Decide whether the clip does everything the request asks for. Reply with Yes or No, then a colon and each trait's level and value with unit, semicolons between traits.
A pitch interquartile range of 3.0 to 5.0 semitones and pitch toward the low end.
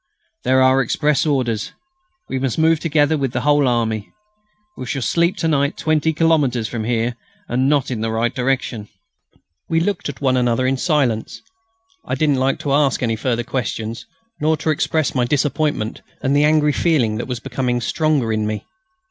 Yes: average, 3.9 semitones; low, 130 Hz